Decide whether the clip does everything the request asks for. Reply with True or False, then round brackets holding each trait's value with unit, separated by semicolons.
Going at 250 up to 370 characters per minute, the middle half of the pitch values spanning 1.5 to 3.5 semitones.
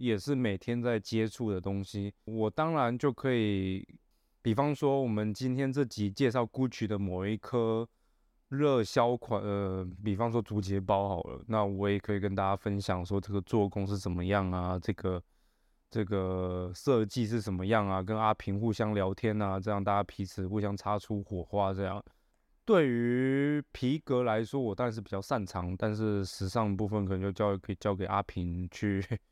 True (270 characters per minute; 2.8 semitones)